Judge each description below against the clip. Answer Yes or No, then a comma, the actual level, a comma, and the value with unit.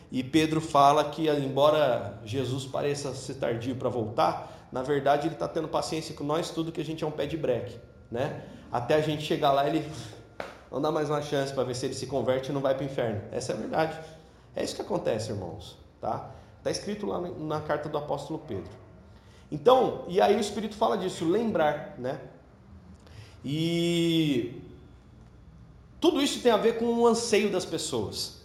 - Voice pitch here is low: No, medium, 150 Hz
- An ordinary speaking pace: No, fast, 190 wpm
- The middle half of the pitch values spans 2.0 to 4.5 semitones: Yes, average, 3.7 semitones